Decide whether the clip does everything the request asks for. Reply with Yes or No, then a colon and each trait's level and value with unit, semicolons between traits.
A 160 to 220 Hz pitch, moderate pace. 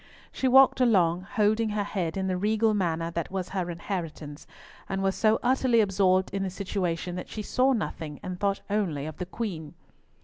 Yes: high, 190 Hz; average, 190 wpm